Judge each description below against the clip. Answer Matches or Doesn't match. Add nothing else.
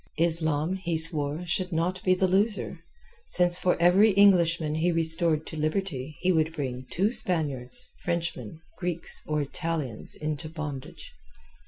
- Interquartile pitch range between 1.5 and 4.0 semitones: Matches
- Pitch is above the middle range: Doesn't match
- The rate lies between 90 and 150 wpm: Matches